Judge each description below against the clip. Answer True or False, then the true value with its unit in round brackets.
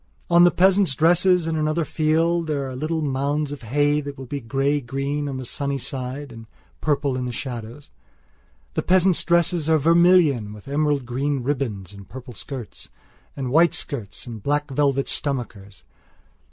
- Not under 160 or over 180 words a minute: True (165 wpm)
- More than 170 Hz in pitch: False (140 Hz)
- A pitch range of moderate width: True (3.4 semitones)